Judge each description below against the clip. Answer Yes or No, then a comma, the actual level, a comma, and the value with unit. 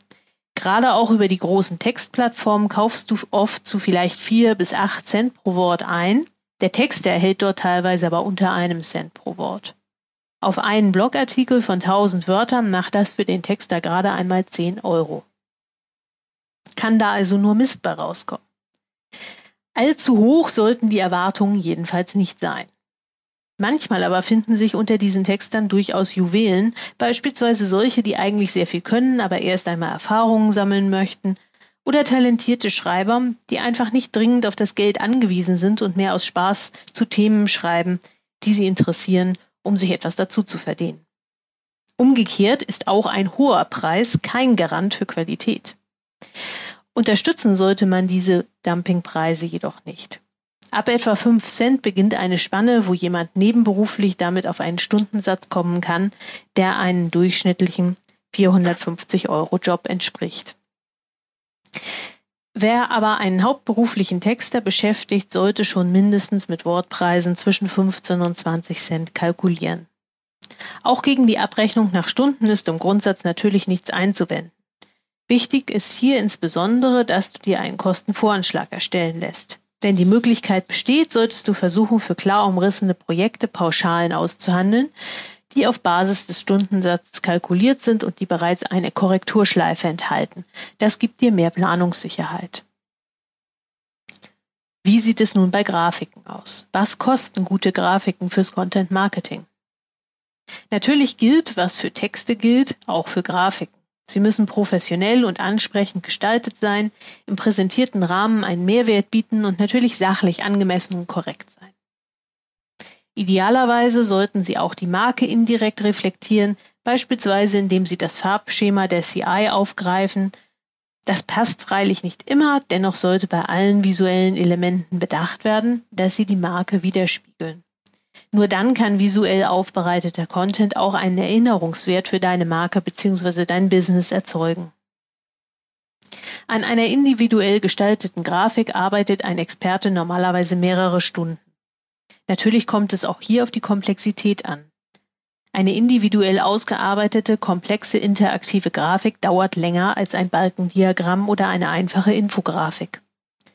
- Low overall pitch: No, high, 195 Hz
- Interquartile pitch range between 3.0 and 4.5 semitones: Yes, average, 3.3 semitones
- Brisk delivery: No, average, 135 wpm